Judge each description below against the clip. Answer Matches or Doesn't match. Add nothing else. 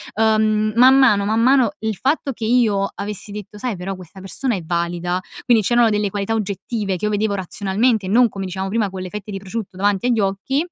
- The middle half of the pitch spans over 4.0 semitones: Doesn't match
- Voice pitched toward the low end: Doesn't match